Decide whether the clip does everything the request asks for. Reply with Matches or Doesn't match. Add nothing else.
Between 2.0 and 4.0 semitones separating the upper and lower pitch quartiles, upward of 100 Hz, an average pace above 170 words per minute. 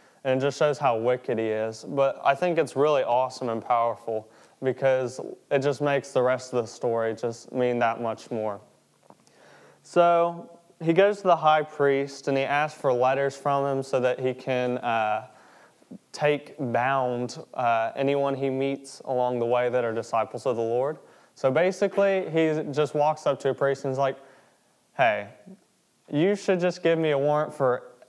Matches